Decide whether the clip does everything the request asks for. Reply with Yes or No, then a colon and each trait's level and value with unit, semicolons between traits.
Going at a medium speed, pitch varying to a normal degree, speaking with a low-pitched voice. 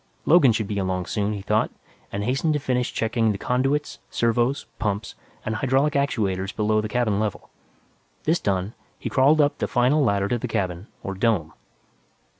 Yes: average, 175 wpm; average, 4.6 semitones; low, 110 Hz